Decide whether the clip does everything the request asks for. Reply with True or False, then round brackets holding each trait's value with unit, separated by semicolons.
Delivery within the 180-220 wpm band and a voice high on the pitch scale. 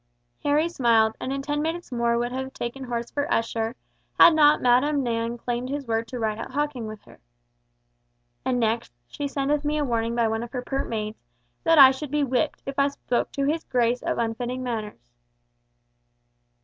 True (190 wpm; 250 Hz)